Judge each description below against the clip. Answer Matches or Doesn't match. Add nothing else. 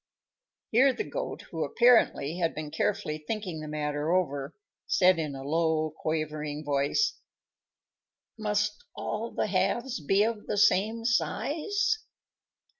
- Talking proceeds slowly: Matches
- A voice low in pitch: Doesn't match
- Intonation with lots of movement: Matches